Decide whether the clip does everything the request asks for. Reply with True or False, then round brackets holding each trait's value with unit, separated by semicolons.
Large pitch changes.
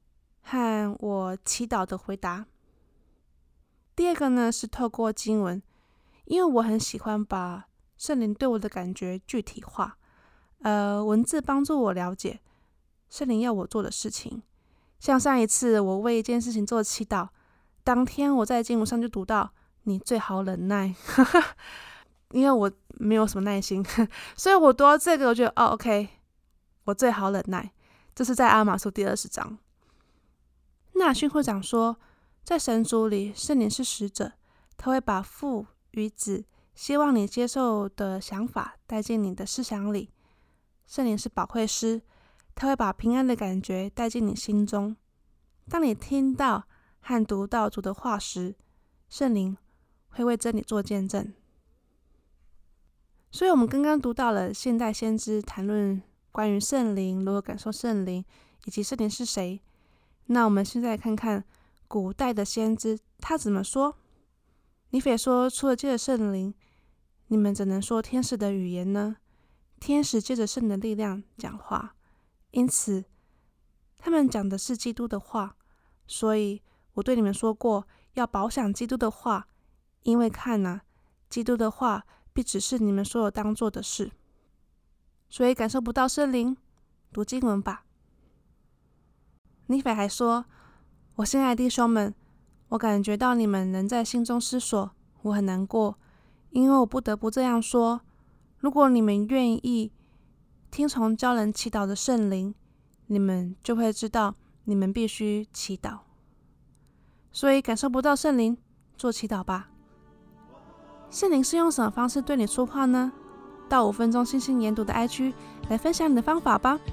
False (3.7 semitones)